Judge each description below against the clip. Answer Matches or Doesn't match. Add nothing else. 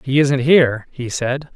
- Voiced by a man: Matches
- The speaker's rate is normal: Matches